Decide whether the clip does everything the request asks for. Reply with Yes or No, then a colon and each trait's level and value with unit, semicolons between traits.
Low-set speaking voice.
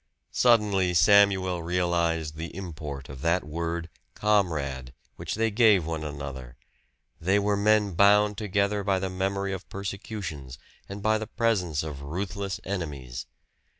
Yes: very low, 95 Hz